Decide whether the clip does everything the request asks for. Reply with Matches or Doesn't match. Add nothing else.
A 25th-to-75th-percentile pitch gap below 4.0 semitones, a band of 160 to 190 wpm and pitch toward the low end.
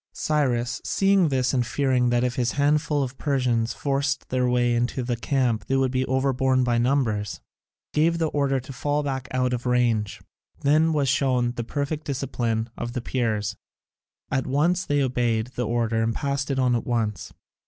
Matches